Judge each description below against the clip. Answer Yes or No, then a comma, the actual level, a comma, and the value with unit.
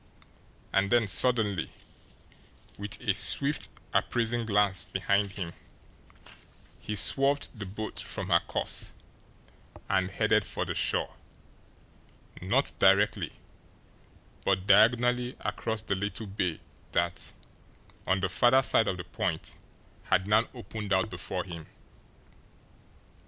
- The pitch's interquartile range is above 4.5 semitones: No, average, 3.2 semitones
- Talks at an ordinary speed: No, slow, 115 wpm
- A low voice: Yes, low, 105 Hz